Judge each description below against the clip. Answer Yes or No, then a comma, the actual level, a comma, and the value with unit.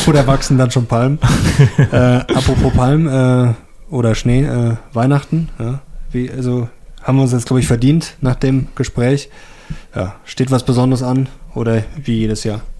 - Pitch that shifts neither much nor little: No, narrow, 2.2 semitones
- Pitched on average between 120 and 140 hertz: Yes, low, 130 Hz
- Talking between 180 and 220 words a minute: No, average, 165 wpm